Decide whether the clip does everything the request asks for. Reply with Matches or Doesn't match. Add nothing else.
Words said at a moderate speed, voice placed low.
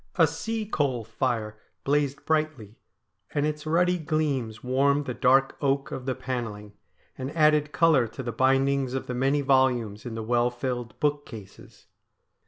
Matches